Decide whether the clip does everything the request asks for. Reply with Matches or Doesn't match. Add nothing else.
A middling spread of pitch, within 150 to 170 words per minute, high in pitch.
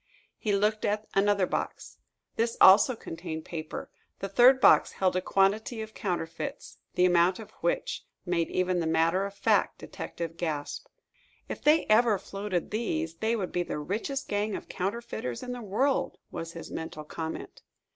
Matches